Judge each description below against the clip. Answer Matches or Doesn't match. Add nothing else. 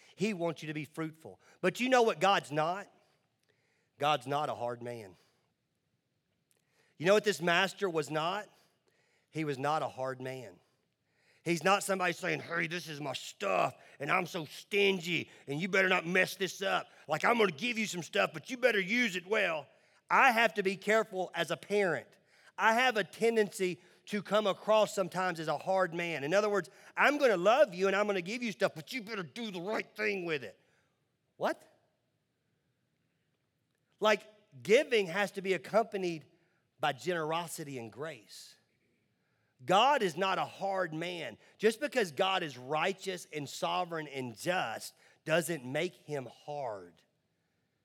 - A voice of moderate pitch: Matches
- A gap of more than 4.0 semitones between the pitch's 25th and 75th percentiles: Matches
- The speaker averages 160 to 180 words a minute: Matches